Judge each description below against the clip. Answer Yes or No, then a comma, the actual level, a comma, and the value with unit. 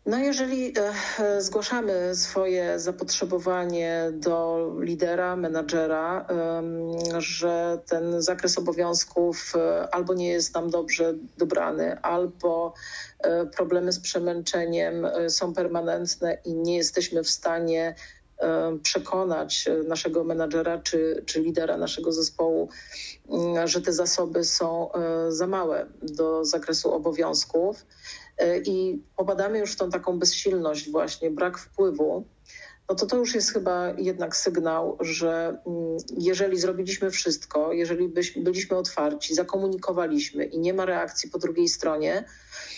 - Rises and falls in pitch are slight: Yes, narrow, 1.9 semitones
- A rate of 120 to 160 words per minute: No, slow, 110 wpm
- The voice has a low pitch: No, medium, 175 Hz